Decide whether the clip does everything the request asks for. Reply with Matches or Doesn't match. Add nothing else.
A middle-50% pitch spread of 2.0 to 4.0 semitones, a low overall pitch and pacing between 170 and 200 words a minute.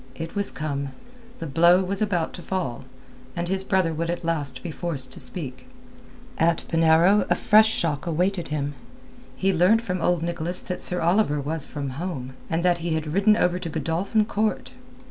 Doesn't match